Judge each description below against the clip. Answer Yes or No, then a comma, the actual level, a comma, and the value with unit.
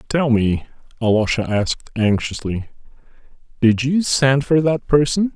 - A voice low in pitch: Yes, low, 130 Hz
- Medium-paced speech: No, slow, 125 wpm